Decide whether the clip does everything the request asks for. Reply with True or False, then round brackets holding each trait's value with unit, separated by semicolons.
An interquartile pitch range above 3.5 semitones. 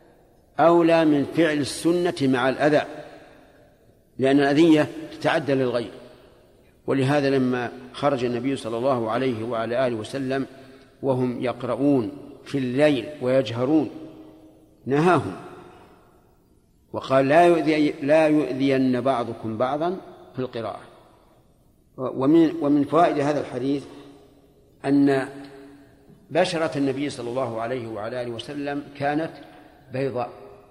False (2.7 semitones)